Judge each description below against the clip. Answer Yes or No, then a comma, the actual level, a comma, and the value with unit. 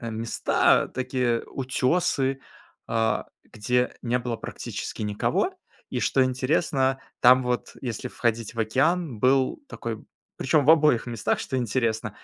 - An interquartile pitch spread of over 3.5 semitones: No, narrow, 2.5 semitones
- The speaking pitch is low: Yes, low, 125 Hz